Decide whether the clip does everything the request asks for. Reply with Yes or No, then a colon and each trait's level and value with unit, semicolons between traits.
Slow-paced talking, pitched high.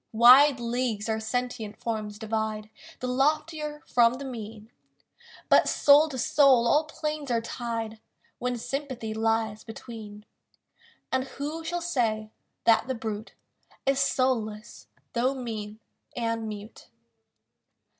Yes: slow, 120 wpm; high, 235 Hz